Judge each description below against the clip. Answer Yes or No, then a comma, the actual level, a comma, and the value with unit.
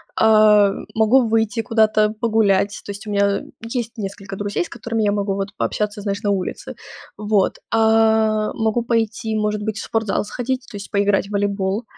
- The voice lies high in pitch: Yes, high, 215 Hz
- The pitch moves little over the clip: Yes, narrow, 1.7 semitones